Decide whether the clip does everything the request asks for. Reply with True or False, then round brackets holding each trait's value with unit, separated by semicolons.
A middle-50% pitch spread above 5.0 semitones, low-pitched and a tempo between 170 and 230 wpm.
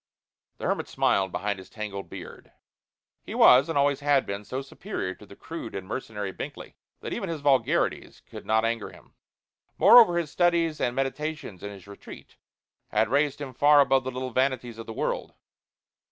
True (5.6 semitones; 130 Hz; 180 wpm)